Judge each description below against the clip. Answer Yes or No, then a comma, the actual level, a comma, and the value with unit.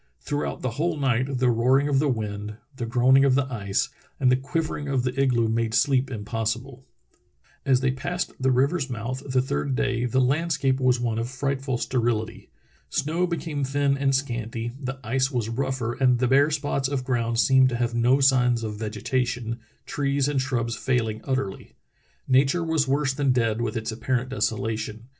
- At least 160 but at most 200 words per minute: Yes, average, 180 wpm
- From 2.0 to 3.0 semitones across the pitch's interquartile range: Yes, average, 2.7 semitones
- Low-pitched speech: Yes, low, 130 Hz